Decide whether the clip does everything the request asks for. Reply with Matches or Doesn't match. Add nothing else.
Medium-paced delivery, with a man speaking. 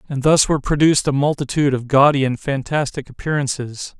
Matches